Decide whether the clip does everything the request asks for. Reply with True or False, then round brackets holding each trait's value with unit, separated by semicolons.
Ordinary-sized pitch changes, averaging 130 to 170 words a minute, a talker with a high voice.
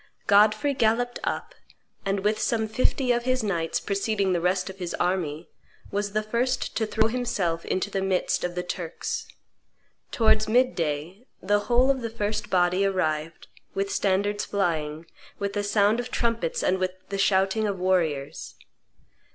True (3.4 semitones; 160 wpm; 200 Hz)